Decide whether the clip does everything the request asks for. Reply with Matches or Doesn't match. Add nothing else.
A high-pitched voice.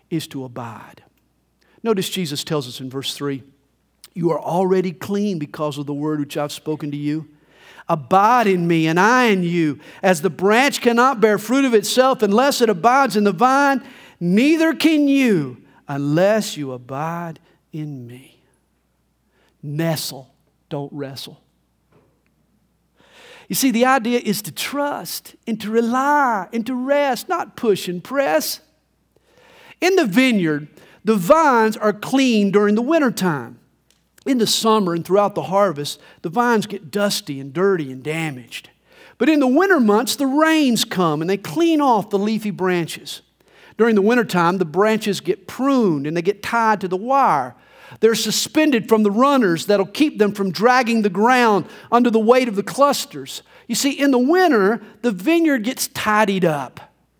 Matches